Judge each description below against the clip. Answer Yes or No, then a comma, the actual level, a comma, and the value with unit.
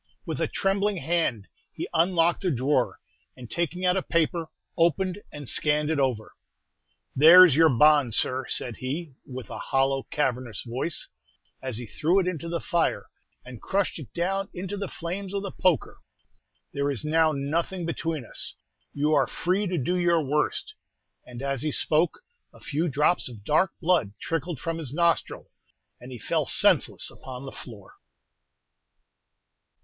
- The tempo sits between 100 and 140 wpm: No, average, 160 wpm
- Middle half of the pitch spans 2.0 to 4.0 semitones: No, average, 4.8 semitones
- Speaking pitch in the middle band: Yes, medium, 155 Hz